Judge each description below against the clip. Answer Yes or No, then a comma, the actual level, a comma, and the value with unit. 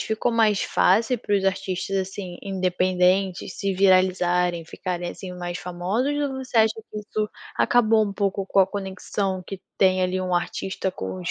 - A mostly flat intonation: Yes, narrow, 2.3 semitones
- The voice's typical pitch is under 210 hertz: Yes, high, 190 Hz